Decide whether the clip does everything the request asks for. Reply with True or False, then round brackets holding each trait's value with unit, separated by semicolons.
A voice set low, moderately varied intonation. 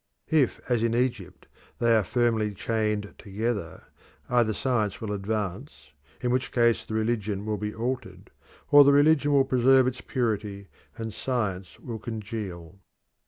True (110 Hz; 3.2 semitones)